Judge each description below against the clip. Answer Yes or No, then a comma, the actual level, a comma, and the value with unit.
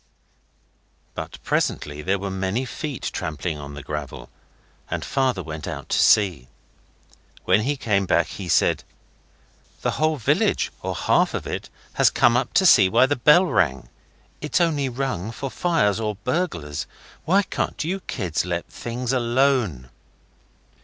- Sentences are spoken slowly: No, average, 150 wpm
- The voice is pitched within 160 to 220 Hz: No, low, 110 Hz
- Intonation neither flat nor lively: No, wide, 8.0 semitones